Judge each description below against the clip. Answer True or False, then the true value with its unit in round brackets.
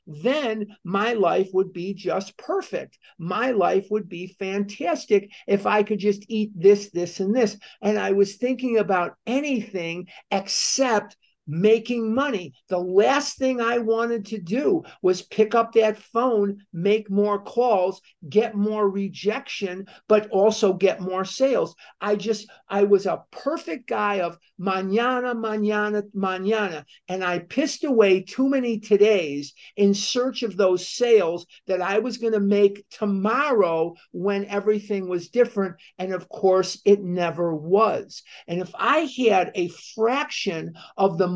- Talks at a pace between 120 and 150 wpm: True (145 wpm)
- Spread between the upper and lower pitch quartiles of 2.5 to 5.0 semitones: True (3.3 semitones)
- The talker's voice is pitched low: False (205 Hz)